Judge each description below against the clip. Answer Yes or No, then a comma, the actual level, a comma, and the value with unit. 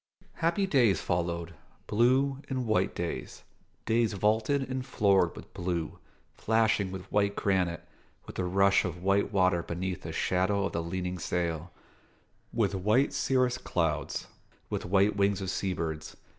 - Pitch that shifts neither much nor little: Yes, average, 4.0 semitones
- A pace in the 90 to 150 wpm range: Yes, average, 145 wpm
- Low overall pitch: Yes, low, 100 Hz